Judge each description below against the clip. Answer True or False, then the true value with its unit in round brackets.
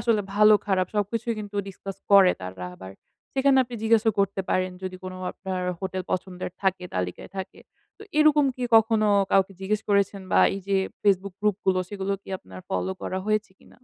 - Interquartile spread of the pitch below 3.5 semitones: True (2.4 semitones)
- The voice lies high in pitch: True (195 Hz)